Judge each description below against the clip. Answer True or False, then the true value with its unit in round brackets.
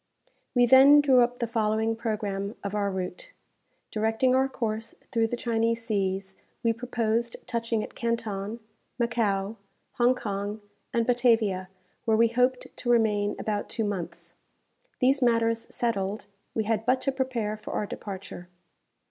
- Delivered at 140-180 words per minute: True (145 wpm)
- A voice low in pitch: False (225 Hz)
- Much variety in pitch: False (2.5 semitones)